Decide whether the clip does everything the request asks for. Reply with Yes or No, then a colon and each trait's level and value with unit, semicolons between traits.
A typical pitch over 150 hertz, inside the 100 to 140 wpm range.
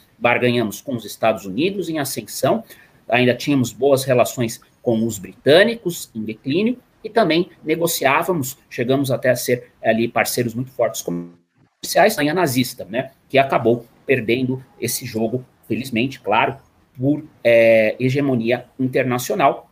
No: low, 125 Hz; average, 130 wpm